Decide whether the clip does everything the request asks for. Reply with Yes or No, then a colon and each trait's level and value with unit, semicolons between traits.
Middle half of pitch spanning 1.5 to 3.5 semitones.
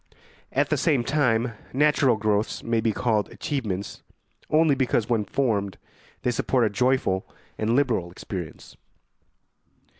No: average, 4.1 semitones